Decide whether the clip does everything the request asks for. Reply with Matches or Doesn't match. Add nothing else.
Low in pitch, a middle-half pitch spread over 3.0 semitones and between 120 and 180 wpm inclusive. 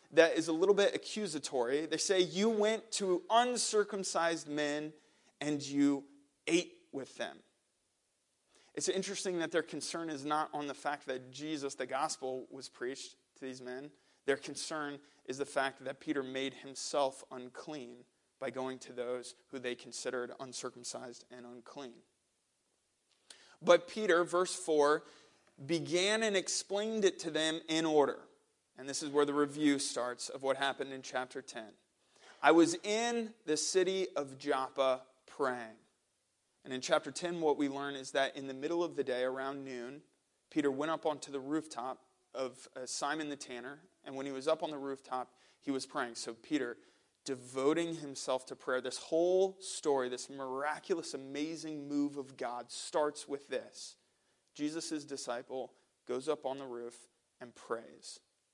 Doesn't match